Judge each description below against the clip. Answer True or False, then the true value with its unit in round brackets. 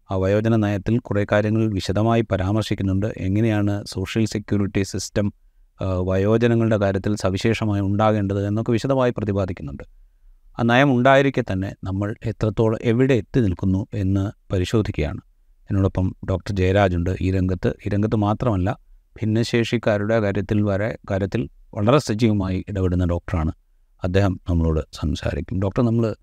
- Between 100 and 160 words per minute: True (110 wpm)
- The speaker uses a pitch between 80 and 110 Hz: True (100 Hz)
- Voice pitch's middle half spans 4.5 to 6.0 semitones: False (2.9 semitones)